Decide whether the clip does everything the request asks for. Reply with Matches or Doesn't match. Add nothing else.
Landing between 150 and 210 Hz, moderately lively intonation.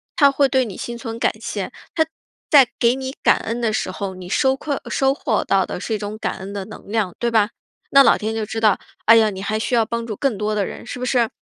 Doesn't match